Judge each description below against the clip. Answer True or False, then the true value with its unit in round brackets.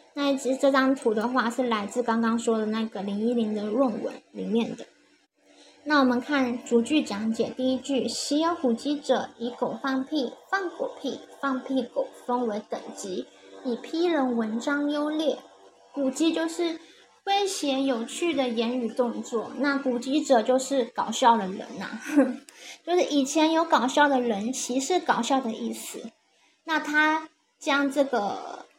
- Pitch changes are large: False (3.6 semitones)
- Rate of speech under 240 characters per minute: True (225 characters per minute)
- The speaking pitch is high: True (260 Hz)